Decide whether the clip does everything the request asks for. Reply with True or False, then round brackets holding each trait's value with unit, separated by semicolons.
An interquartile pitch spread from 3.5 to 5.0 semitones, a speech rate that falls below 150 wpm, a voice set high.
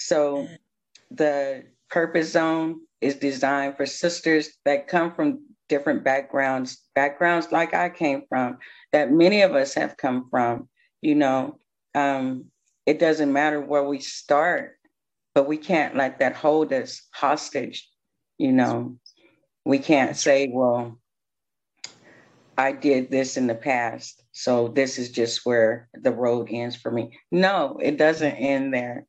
False (4.1 semitones; 140 wpm; 140 Hz)